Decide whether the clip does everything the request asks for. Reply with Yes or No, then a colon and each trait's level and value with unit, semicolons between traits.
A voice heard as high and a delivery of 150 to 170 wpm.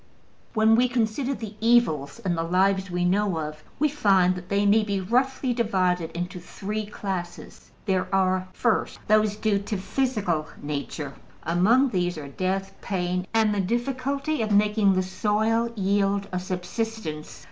Yes: high, 200 Hz; average, 155 wpm